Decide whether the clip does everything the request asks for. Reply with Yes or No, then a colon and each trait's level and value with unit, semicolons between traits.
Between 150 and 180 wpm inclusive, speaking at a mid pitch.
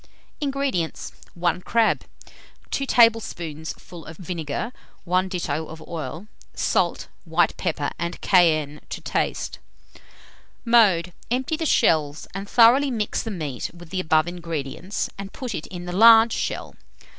No: slow, 135 wpm; medium, 180 Hz